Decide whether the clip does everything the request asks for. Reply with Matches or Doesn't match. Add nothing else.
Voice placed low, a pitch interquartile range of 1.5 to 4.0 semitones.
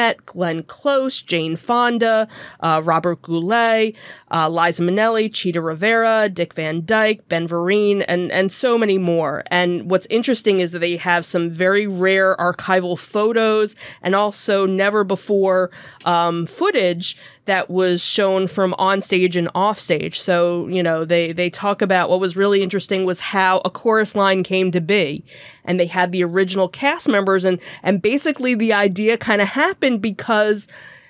Doesn't match